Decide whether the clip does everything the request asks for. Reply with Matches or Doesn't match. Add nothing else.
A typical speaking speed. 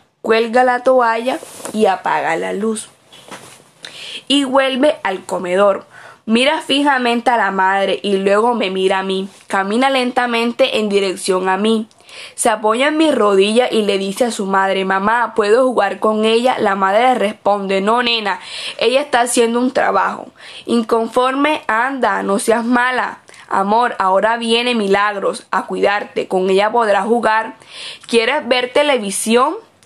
Matches